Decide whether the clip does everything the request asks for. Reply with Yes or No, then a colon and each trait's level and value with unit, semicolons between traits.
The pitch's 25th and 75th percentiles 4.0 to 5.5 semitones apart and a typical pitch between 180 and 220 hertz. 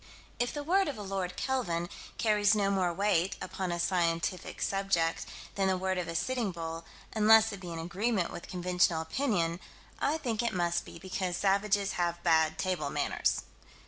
No: average, 3.5 semitones; medium, 185 Hz